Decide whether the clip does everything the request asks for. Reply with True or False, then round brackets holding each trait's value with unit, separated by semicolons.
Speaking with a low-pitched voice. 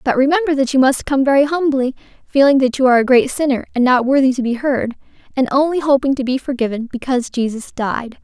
False (265 Hz)